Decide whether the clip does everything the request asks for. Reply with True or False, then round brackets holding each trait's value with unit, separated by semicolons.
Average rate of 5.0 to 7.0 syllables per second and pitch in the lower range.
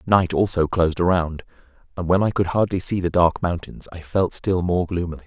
True (5.5 syllables/s; 90 Hz)